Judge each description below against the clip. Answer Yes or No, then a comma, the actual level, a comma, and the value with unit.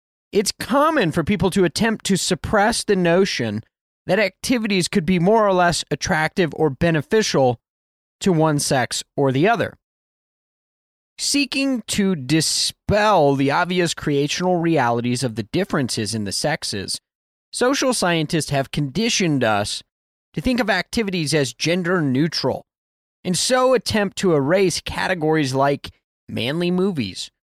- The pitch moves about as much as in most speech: No, wide, 6.5 semitones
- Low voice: No, medium, 170 Hz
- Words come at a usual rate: No, slow, 130 wpm